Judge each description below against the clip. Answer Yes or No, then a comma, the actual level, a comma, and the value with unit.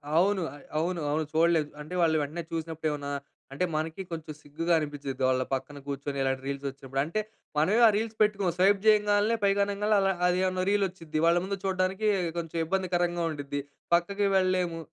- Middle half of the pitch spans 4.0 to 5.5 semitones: Yes, average, 4.4 semitones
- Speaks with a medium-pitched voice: Yes, medium, 170 Hz